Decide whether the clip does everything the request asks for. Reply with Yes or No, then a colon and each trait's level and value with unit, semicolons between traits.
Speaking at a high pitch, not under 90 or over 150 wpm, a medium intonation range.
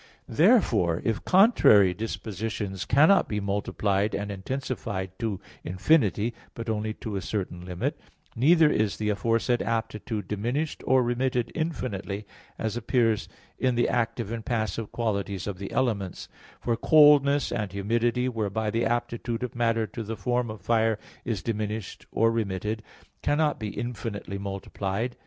No: low, 110 Hz; average, 140 wpm; average, 3.1 semitones